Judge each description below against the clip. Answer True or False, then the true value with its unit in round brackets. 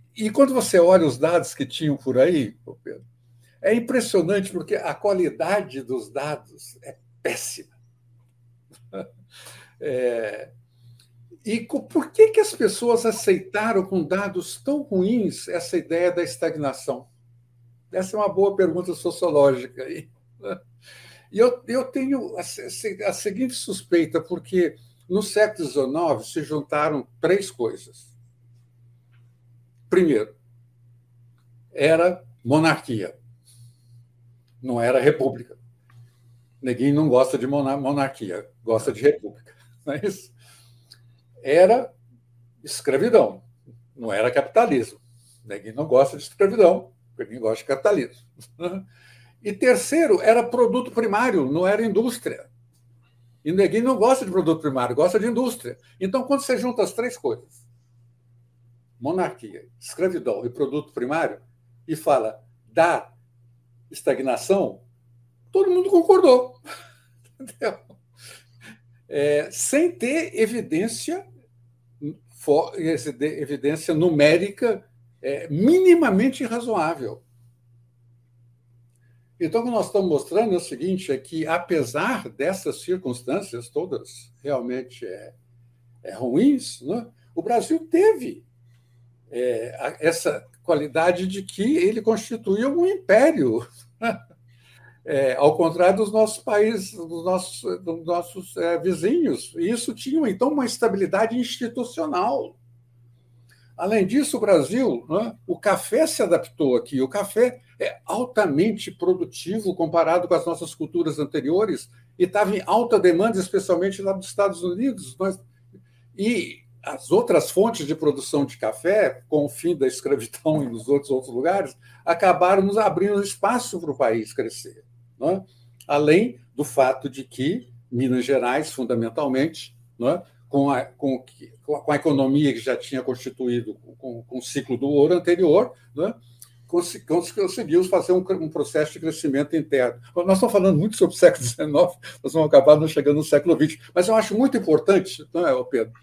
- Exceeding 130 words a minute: False (125 wpm)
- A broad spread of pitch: True (8.3 semitones)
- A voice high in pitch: False (150 Hz)